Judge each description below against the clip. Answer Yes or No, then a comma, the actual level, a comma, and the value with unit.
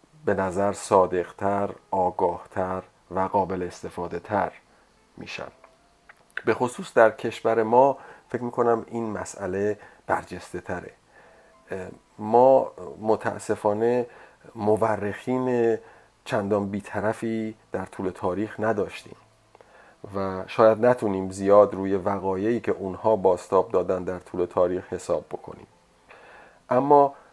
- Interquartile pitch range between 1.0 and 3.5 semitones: Yes, average, 3.1 semitones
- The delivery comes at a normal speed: No, slow, 95 wpm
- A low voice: Yes, low, 105 Hz